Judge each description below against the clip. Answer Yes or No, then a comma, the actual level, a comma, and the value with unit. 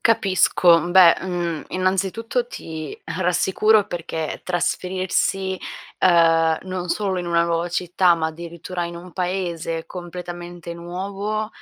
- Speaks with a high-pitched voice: No, medium, 175 Hz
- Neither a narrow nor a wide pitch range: No, narrow, 1.8 semitones